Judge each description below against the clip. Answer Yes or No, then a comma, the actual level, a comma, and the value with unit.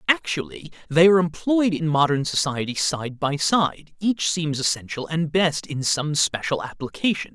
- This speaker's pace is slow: No, average, 155 wpm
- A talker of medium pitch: Yes, medium, 160 Hz